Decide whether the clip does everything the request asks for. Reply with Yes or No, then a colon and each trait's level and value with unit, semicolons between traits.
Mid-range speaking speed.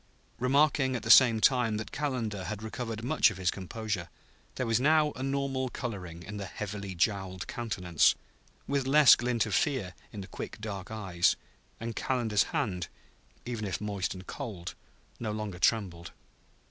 Yes: average, 160 wpm